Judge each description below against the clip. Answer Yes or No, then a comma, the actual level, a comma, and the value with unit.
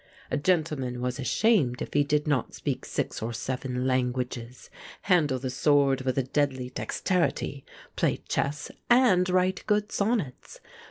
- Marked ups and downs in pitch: Yes, wide, 6.1 semitones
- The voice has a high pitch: No, medium, 140 Hz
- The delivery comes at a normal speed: Yes, average, 145 wpm